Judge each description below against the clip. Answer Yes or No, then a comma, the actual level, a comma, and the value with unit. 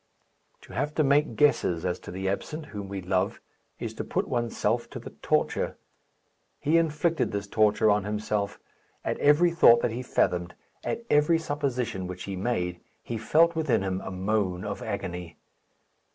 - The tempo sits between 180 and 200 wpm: No, average, 165 wpm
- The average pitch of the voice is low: Yes, low, 105 Hz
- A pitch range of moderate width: No, wide, 7.6 semitones